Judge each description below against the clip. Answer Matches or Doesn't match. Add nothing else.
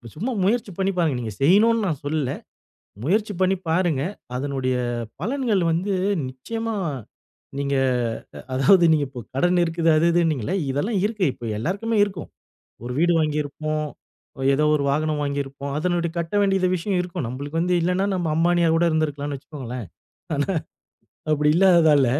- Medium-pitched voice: Matches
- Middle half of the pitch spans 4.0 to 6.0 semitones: Matches